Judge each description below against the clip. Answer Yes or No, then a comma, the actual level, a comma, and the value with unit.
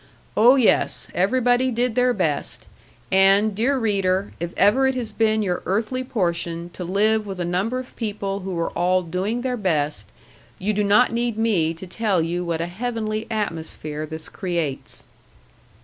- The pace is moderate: Yes, average, 165 wpm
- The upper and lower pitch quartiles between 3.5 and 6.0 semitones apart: Yes, average, 4.5 semitones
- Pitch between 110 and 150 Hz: No, high, 200 Hz